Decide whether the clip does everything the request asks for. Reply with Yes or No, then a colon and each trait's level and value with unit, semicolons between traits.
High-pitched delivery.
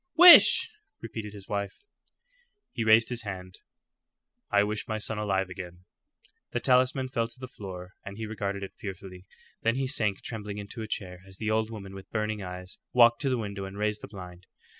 No: low, 105 Hz